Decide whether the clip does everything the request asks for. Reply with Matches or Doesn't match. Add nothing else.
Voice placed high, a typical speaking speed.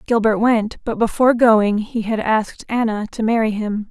Matches